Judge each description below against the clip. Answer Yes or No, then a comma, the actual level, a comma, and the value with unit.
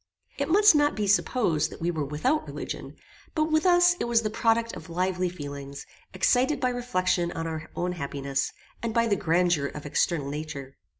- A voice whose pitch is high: No, medium, 180 Hz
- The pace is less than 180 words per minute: No, average, 185 wpm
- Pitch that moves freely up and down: Yes, wide, 8.1 semitones